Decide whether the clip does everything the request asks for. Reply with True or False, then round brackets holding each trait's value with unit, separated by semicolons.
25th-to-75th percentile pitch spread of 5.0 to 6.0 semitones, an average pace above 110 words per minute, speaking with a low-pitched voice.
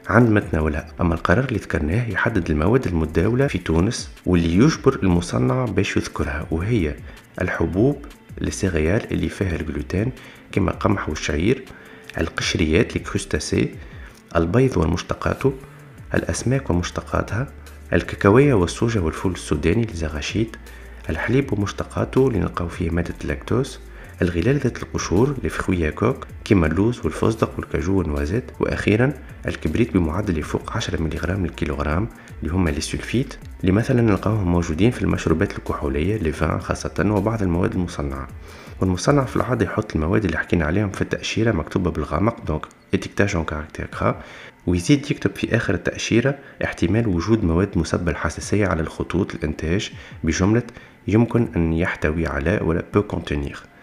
True (5.3 semitones; 120 wpm; 90 Hz)